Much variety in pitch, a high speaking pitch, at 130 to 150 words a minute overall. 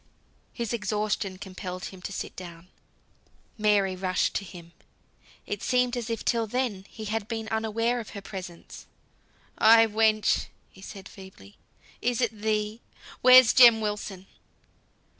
No: average, 3.1 semitones; high, 210 Hz; average, 140 wpm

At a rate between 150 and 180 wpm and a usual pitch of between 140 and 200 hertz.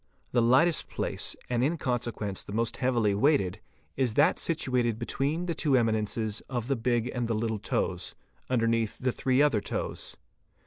No: average, 165 wpm; low, 120 Hz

